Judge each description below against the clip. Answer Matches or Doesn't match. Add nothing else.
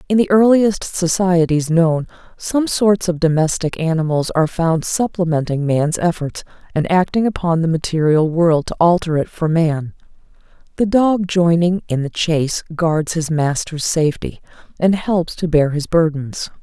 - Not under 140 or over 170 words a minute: Matches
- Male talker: Doesn't match